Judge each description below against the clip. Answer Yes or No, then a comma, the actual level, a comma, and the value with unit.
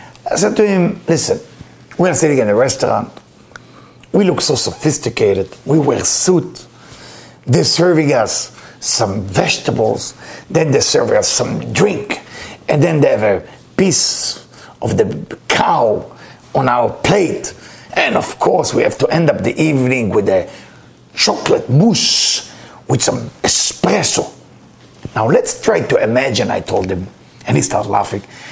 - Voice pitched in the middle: Yes, medium, 180 Hz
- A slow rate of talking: No, average, 145 wpm